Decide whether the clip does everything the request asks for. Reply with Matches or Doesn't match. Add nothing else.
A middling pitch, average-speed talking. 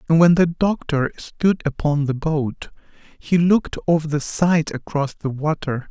Matches